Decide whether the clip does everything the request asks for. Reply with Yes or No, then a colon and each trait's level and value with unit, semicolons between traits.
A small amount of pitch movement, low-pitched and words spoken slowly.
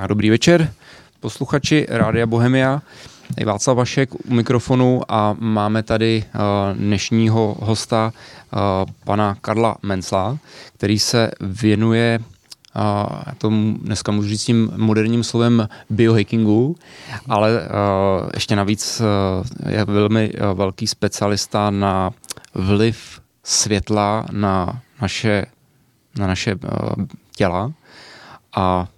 Yes: narrow, 2.3 semitones; low, 110 Hz; slow, 90 wpm